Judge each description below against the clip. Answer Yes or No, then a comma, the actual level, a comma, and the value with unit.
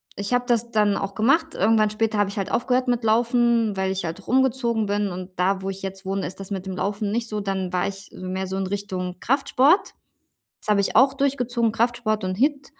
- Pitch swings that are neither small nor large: Yes, average, 3.8 semitones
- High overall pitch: Yes, high, 210 Hz